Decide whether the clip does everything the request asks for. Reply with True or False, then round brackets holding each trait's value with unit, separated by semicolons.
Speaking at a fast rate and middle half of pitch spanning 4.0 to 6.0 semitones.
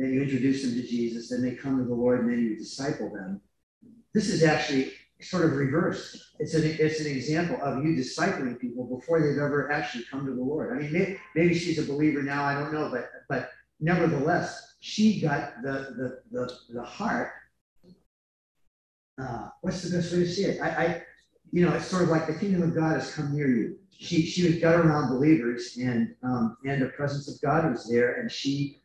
True (210 wpm; 4.8 semitones)